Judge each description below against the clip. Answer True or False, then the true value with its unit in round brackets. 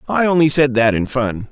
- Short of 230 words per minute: False (240 wpm)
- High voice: False (135 Hz)